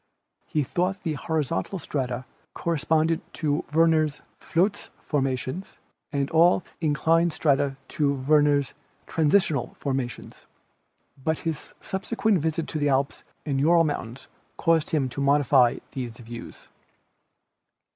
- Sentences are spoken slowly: Yes, slow, 115 wpm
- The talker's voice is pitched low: No, medium, 150 Hz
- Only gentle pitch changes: No, average, 3.2 semitones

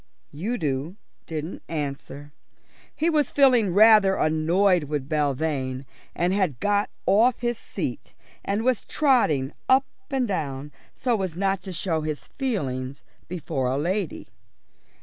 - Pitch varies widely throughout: Yes, wide, 6.6 semitones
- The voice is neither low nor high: Yes, medium, 175 Hz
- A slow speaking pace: Yes, slow, 130 wpm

